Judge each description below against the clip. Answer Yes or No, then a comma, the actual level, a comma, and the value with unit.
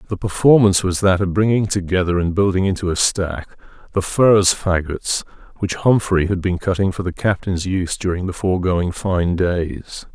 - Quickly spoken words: No, average, 170 wpm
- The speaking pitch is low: Yes, very low, 95 Hz